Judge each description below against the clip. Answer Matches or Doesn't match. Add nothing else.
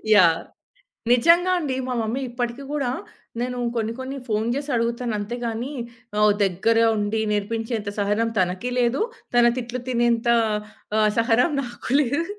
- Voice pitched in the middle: Doesn't match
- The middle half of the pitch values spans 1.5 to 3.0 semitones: Matches